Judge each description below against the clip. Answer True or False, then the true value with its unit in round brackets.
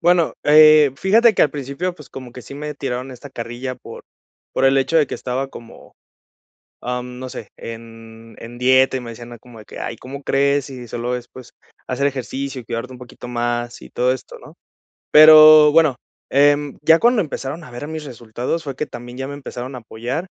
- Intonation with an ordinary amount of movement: True (3.2 semitones)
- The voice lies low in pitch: True (130 Hz)